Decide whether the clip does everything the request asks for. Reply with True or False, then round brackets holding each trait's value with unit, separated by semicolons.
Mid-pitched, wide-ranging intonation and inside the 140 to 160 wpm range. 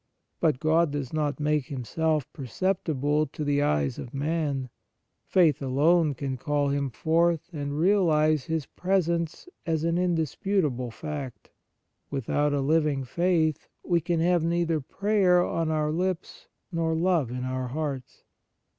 False (155 Hz; 3.2 semitones; 145 wpm)